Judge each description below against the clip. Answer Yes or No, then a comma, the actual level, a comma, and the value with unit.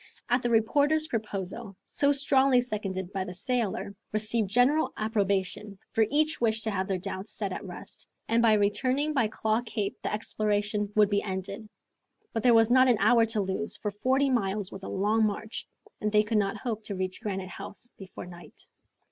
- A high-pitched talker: Yes, high, 215 Hz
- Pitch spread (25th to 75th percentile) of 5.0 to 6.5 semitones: No, average, 3.2 semitones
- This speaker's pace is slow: No, average, 185 wpm